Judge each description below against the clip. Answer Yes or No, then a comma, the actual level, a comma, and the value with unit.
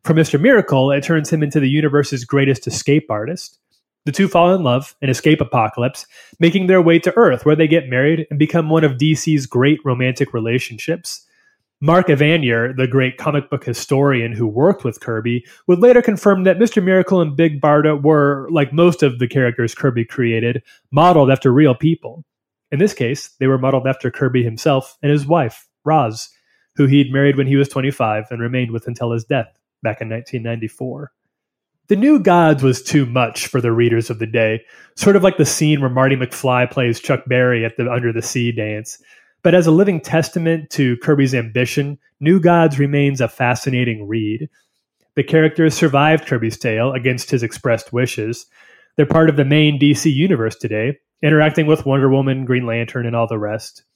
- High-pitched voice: No, medium, 140 Hz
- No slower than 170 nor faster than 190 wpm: Yes, average, 185 wpm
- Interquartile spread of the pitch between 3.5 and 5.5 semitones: Yes, average, 4.2 semitones